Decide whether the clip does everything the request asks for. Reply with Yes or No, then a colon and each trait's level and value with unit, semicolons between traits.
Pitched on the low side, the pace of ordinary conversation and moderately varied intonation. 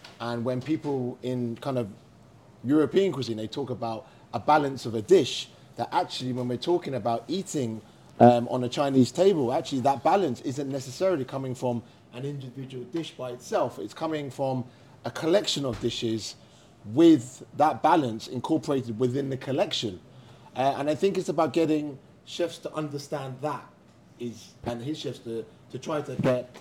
Yes: low, 130 Hz; average, 165 wpm; average, 3.9 semitones